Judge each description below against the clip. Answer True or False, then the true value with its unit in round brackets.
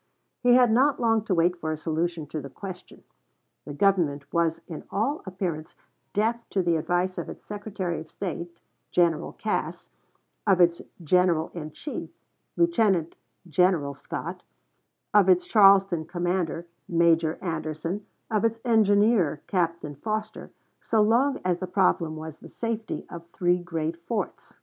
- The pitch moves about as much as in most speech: True (4.3 semitones)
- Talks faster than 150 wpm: False (145 wpm)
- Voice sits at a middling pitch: True (180 Hz)